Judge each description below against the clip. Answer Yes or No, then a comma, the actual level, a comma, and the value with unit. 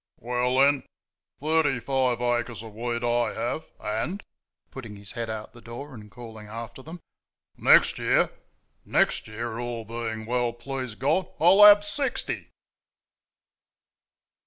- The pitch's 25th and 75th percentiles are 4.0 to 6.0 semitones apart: No, average, 3.1 semitones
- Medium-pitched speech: No, low, 120 Hz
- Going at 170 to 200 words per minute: No, slow, 135 wpm